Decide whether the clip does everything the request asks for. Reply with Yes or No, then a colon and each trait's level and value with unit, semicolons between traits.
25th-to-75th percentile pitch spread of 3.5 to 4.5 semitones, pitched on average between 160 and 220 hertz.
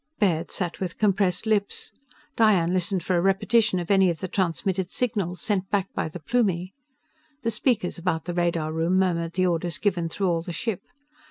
No: average, 2.9 semitones; medium, 185 Hz